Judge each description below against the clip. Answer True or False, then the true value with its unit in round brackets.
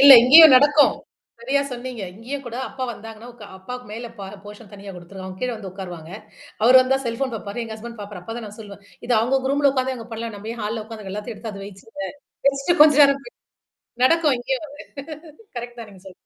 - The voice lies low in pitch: False (230 Hz)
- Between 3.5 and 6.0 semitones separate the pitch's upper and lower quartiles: True (4.2 semitones)